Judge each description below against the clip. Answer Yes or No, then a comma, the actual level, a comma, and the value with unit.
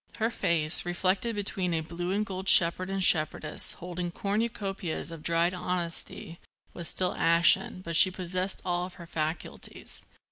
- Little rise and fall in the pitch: Yes, narrow, 2.0 semitones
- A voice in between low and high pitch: Yes, medium, 180 Hz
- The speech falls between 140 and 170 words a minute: Yes, average, 145 wpm